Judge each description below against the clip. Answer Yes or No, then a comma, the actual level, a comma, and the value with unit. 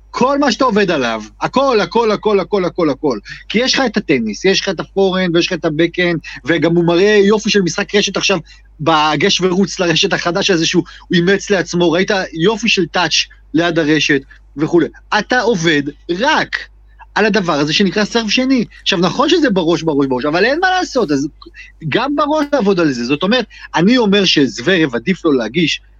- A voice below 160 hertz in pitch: No, medium, 185 Hz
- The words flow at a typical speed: No, fast, 185 wpm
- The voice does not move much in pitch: No, average, 4.2 semitones